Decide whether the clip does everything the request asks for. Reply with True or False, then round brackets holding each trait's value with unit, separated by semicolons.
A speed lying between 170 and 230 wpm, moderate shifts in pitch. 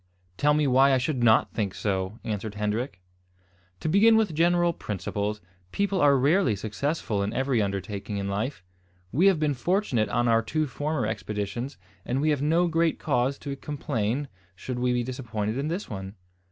False (175 wpm; 6.2 semitones)